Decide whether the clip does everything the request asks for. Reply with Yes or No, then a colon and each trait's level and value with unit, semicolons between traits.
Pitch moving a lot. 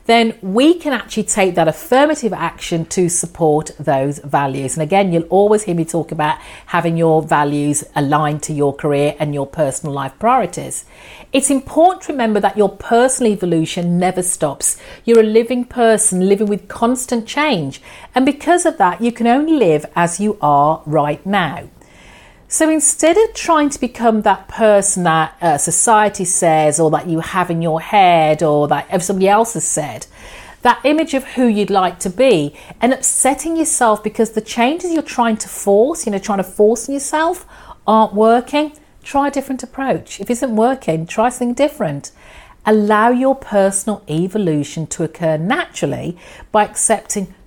Yes: wide, 7.2 semitones